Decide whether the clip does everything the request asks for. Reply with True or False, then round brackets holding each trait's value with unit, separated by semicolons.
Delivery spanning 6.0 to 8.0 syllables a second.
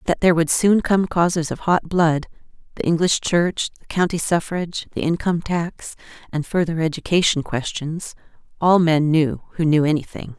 False (5.0 syllables/s)